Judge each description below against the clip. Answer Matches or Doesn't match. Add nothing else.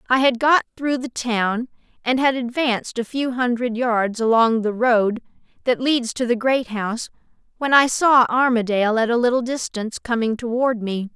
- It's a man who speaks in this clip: Doesn't match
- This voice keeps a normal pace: Matches